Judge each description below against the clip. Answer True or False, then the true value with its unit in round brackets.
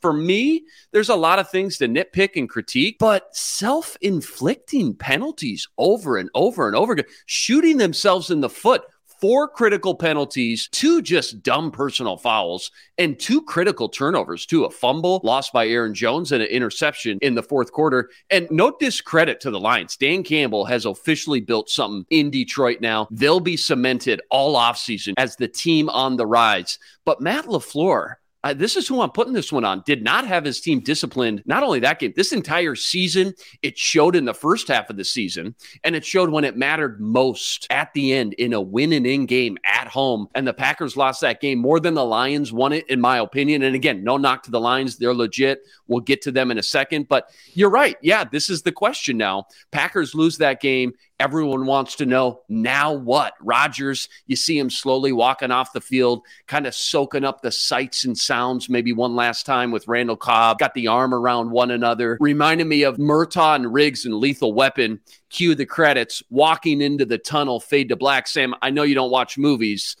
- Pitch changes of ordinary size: False (6.1 semitones)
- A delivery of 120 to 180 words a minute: False (200 wpm)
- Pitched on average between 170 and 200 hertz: False (140 Hz)